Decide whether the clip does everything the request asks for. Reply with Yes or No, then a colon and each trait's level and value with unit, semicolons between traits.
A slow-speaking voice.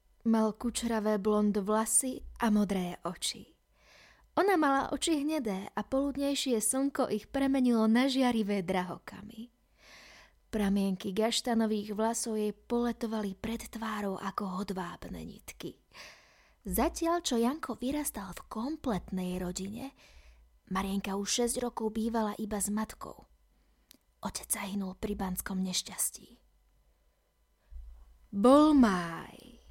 Yes: slow, 105 wpm